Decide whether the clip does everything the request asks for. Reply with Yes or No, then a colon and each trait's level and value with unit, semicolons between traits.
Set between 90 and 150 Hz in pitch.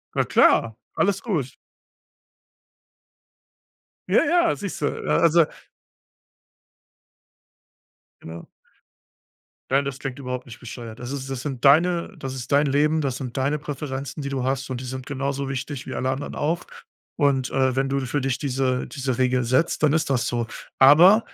Yes: low, 135 Hz